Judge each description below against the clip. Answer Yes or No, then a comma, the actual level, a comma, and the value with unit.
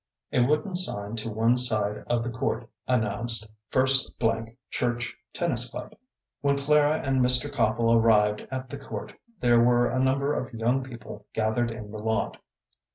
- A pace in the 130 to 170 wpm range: Yes, average, 160 wpm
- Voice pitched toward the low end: Yes, low, 120 Hz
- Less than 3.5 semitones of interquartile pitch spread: Yes, average, 2.9 semitones